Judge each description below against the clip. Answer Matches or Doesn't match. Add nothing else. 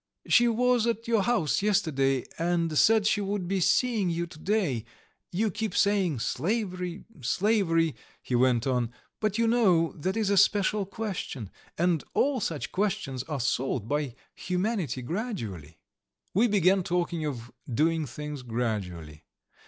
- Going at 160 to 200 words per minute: Doesn't match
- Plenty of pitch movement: Matches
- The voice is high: Doesn't match